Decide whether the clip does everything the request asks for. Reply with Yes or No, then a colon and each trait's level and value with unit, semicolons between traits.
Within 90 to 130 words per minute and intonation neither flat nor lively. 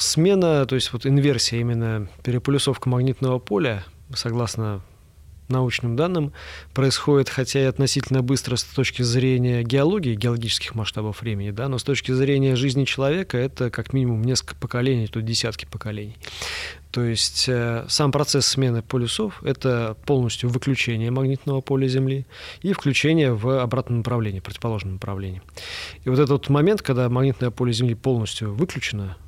No: average, 145 wpm; average, 3.2 semitones